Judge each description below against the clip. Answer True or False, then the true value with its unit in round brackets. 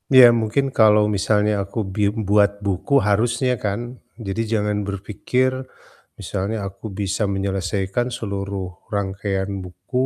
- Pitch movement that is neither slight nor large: False (1.9 semitones)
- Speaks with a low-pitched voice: True (100 Hz)